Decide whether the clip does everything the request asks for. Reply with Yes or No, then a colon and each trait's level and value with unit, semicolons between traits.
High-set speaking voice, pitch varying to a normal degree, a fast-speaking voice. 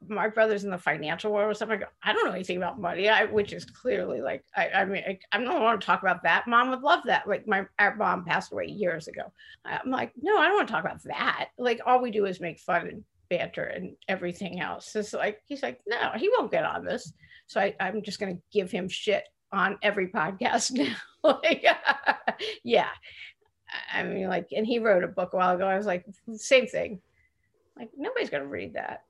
No: high, 220 Hz; wide, 6.5 semitones; fast, 230 wpm